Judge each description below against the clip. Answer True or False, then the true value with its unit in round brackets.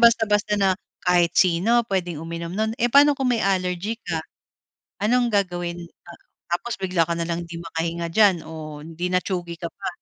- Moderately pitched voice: True (180 Hz)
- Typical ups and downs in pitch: True (3.7 semitones)